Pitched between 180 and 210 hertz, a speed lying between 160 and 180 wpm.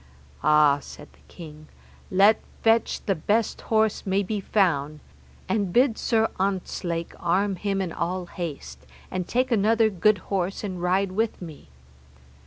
No: high, 190 Hz; average, 145 wpm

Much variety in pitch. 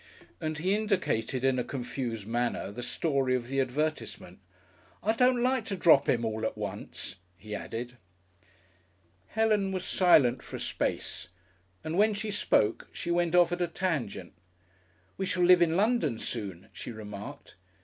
Yes: wide, 7.9 semitones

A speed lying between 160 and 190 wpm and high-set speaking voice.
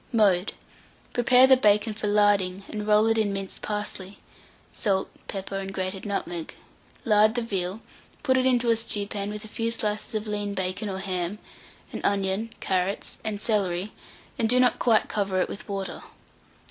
Yes: average, 170 wpm; high, 205 Hz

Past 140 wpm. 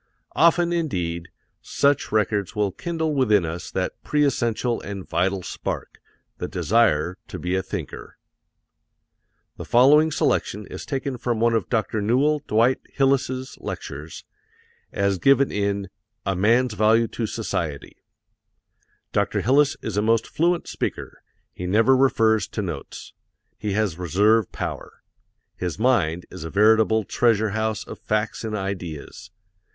No: slow, 135 wpm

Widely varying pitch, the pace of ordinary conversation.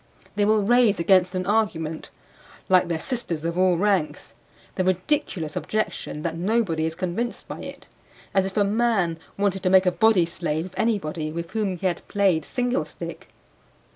No: average, 3.9 semitones; average, 170 wpm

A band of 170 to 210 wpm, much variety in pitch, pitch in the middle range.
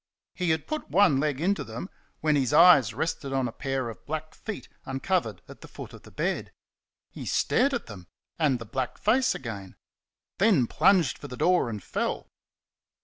Yes: average, 185 wpm; wide, 6.4 semitones; medium, 145 Hz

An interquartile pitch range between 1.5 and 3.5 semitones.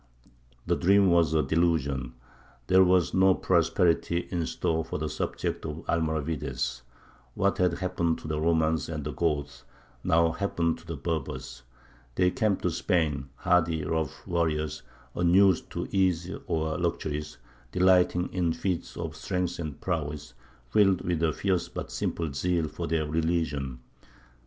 Yes: average, 2.7 semitones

